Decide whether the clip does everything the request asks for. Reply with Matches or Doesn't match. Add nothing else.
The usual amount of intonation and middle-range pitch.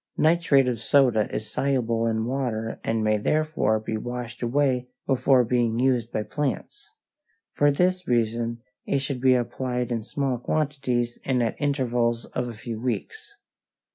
Doesn't match